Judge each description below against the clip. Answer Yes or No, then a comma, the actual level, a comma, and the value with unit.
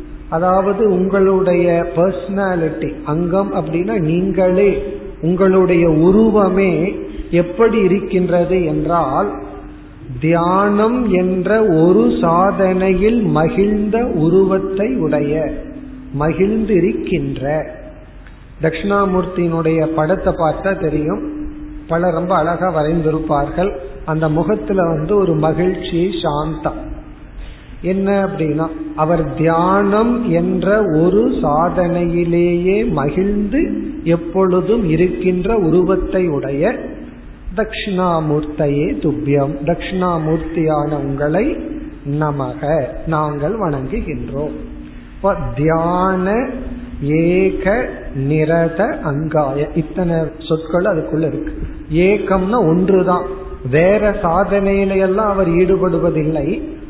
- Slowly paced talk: Yes, slow, 70 wpm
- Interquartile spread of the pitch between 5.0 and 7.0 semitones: No, average, 3.7 semitones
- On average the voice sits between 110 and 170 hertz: No, medium, 180 Hz